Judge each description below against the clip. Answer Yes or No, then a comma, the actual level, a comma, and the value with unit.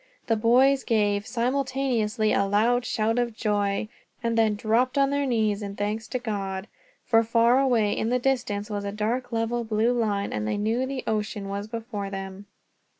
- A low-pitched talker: No, high, 220 Hz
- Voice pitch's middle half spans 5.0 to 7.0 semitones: No, average, 3.0 semitones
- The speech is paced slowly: No, average, 180 wpm